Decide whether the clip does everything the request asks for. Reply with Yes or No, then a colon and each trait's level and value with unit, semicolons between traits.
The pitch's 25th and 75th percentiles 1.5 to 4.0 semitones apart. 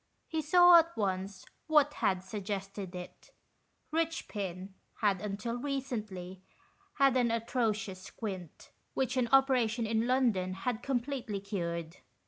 No: wide, 5.5 semitones